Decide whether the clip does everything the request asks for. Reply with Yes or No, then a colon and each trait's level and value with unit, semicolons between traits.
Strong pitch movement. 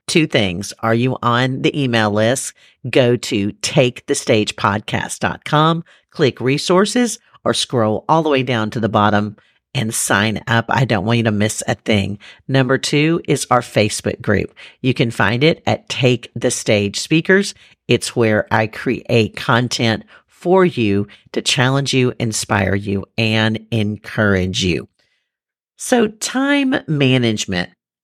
No: average, 4.2 semitones